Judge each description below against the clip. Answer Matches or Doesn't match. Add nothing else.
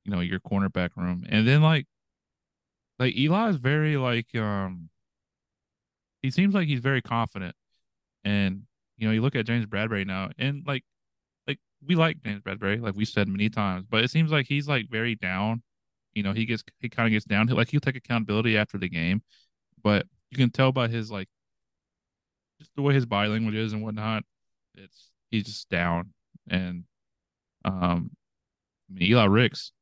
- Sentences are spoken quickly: Doesn't match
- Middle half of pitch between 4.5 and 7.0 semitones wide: Matches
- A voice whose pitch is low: Matches